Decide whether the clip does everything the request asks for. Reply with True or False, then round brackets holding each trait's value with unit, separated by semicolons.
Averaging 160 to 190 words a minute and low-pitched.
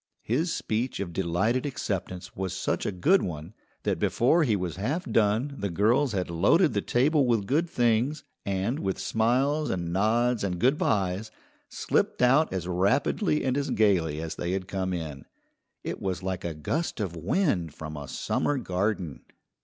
True (170 wpm; 105 Hz)